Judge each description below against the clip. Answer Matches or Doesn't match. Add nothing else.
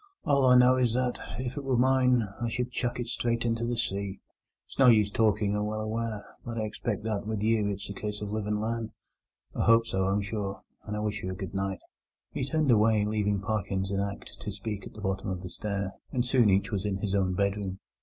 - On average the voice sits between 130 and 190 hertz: Doesn't match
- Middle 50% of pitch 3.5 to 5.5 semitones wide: Doesn't match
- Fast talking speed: Matches